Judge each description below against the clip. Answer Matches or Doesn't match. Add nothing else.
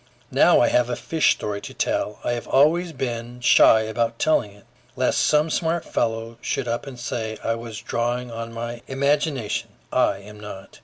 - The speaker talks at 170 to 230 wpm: Matches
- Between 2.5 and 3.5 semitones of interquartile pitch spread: Matches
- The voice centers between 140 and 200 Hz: Doesn't match